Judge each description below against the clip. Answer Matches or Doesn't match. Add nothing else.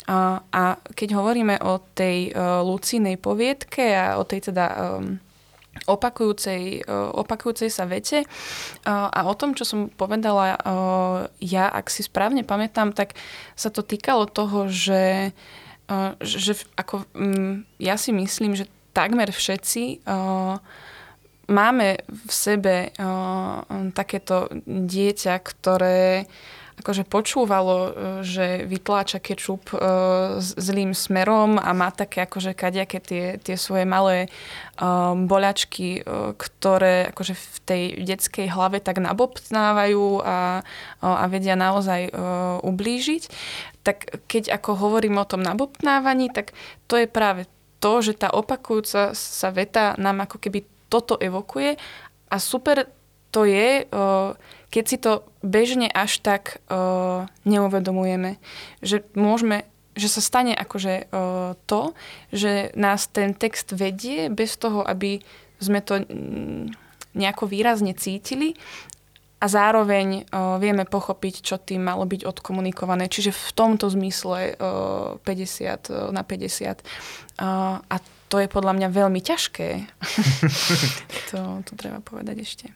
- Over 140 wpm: Doesn't match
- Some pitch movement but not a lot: Doesn't match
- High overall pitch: Matches